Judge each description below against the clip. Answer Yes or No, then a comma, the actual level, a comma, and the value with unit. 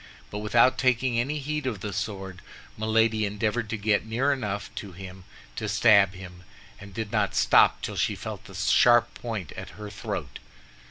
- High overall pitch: No, low, 110 Hz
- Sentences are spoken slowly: No, average, 175 wpm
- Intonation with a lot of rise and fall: No, average, 2.9 semitones